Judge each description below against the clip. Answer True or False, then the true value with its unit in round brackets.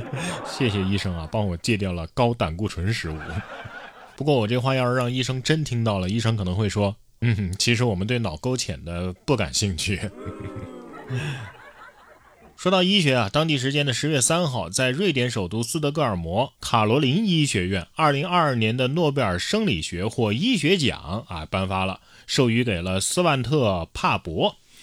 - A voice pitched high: False (115 Hz)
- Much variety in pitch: True (5.8 semitones)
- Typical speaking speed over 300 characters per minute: False (265 characters per minute)